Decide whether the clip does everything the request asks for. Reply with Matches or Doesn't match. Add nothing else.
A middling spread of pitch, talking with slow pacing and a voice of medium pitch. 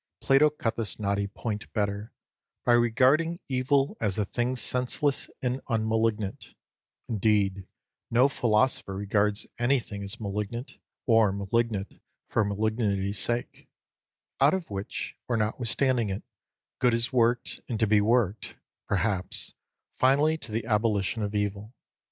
Doesn't match